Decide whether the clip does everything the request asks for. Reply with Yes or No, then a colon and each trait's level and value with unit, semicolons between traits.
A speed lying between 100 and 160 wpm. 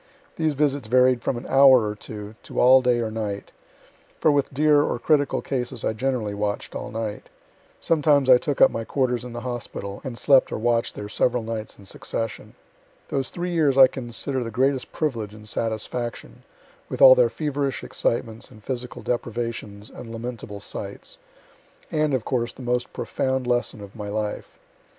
No: average, 175 wpm